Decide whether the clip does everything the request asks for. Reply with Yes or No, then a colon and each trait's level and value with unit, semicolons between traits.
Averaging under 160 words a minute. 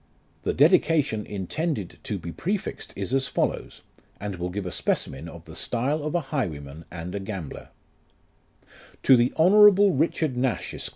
No: average, 165 wpm